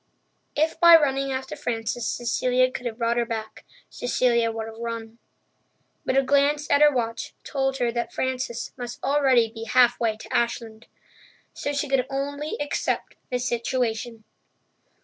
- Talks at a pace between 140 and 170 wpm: Yes, average, 150 wpm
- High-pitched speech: Yes, high, 245 Hz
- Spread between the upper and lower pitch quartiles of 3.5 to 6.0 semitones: No, average, 2.8 semitones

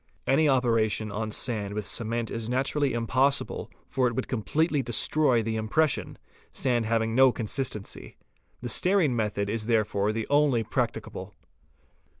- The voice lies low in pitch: Yes, low, 115 Hz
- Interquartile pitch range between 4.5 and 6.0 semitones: No, average, 3.5 semitones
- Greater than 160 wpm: No, average, 145 wpm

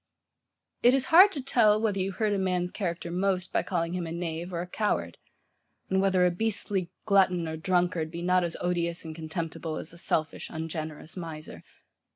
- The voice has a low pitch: No, medium, 180 Hz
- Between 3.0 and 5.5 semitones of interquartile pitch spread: No, narrow, 2.6 semitones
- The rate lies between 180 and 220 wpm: Yes, average, 190 wpm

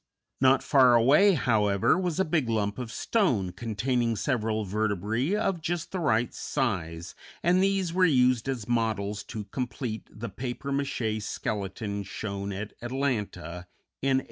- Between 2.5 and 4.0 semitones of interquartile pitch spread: No, average, 4.9 semitones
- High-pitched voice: No, low, 120 Hz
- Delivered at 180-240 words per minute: No, average, 145 wpm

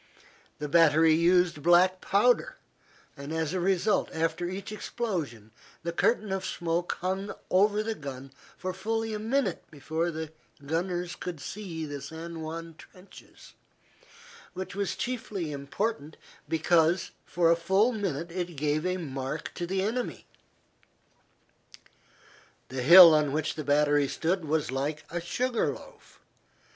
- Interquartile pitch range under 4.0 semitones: Yes, average, 3.6 semitones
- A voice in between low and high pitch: Yes, medium, 170 Hz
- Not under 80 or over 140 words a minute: Yes, slow, 135 wpm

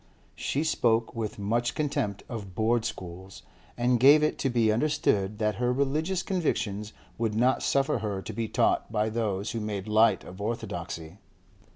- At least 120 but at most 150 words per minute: No, average, 165 wpm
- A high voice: No, low, 110 Hz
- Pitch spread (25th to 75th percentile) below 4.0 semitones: Yes, average, 3.3 semitones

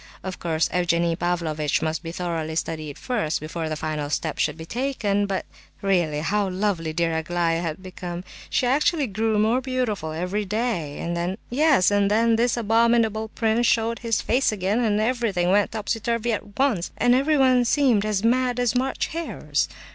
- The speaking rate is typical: Yes, average, 165 wpm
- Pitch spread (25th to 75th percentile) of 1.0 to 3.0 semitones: No, wide, 5.6 semitones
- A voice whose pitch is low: No, high, 205 Hz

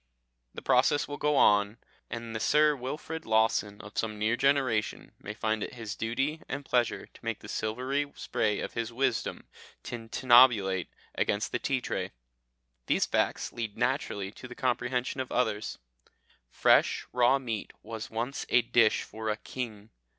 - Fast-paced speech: No, average, 160 wpm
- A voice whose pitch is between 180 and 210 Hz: No, low, 115 Hz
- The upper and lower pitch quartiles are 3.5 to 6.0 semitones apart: No, average, 3.0 semitones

